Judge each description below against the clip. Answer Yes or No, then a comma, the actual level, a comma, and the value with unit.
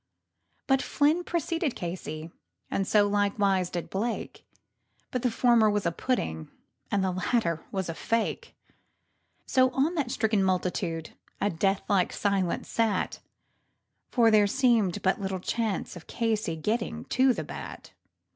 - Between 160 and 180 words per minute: No, average, 140 wpm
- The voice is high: Yes, high, 205 Hz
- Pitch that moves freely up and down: No, average, 4.4 semitones